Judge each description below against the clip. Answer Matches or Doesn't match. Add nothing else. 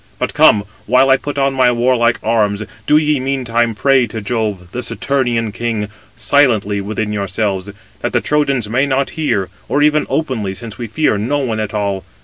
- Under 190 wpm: Matches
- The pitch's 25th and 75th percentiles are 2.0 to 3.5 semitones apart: Doesn't match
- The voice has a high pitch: Doesn't match